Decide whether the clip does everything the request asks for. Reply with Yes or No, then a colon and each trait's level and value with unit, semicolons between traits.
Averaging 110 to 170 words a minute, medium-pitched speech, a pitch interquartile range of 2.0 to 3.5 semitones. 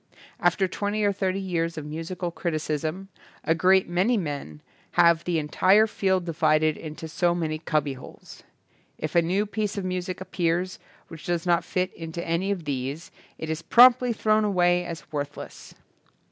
Yes: average, 160 wpm; medium, 175 Hz; average, 3.1 semitones